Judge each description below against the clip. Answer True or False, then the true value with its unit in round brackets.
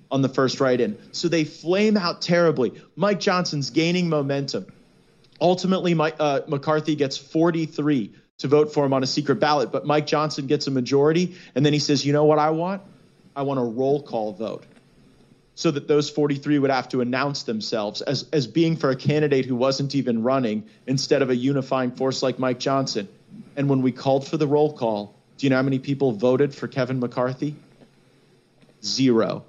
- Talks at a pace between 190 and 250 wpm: True (195 wpm)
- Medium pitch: True (145 Hz)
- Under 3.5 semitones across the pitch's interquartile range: True (2.8 semitones)